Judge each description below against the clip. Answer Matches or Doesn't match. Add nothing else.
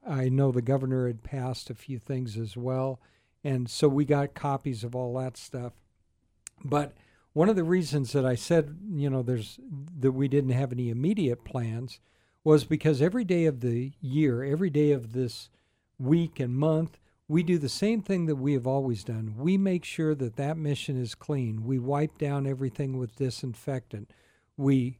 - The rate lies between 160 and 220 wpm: Matches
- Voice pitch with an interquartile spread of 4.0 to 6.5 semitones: Doesn't match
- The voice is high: Doesn't match